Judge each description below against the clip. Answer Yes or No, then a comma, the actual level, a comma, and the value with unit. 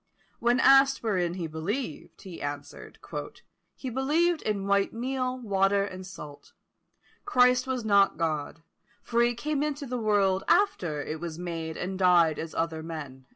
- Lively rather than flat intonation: Yes, wide, 7.3 semitones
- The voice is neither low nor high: No, high, 195 Hz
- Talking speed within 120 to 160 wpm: Yes, average, 155 wpm